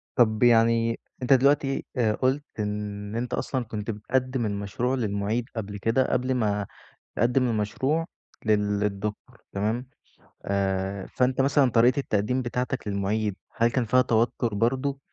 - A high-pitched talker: No, low, 115 Hz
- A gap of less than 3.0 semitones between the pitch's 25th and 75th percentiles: No, average, 3.6 semitones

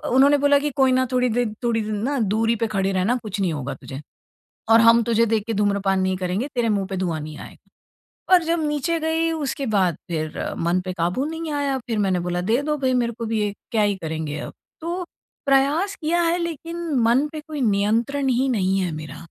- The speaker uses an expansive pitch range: Yes, wide, 7.0 semitones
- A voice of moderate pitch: No, high, 230 Hz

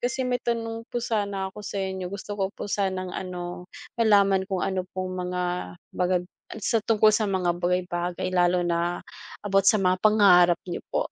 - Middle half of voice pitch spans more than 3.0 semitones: No, narrow, 2.5 semitones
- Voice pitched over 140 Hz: Yes, high, 190 Hz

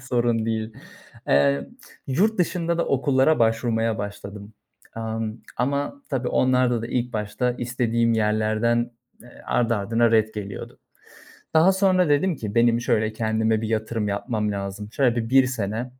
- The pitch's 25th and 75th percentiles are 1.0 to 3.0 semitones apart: Yes, average, 2.7 semitones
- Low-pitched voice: Yes, low, 115 Hz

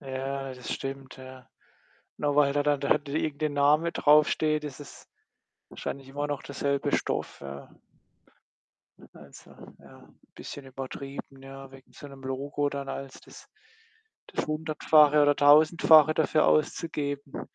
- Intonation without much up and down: Yes, narrow, 1.7 semitones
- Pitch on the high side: No, medium, 140 Hz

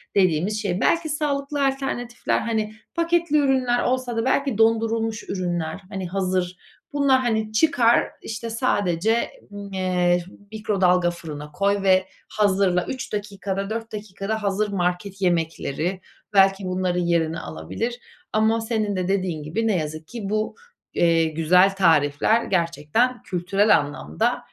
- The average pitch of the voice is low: No, high, 195 Hz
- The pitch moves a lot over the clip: No, average, 4.3 semitones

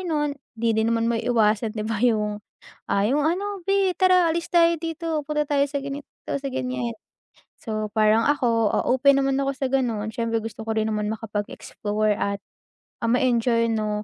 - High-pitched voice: Yes, high, 245 Hz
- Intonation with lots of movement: No, average, 4.9 semitones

